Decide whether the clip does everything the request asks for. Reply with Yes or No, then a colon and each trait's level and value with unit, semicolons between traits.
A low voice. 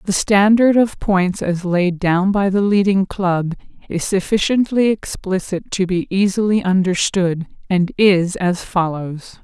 No: high, 190 Hz